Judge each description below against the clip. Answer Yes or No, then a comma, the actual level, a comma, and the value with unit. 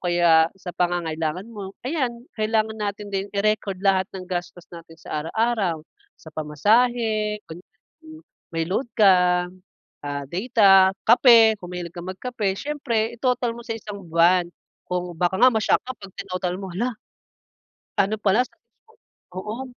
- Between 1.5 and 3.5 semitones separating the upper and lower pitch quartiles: No, average, 4.1 semitones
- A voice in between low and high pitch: No, high, 195 Hz